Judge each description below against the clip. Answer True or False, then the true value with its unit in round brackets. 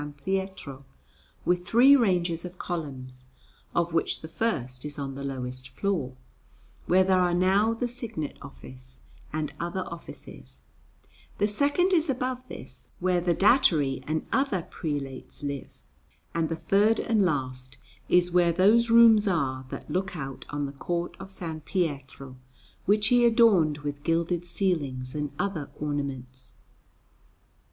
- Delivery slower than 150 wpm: True (140 wpm)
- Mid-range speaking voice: True (170 Hz)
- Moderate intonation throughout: False (6.0 semitones)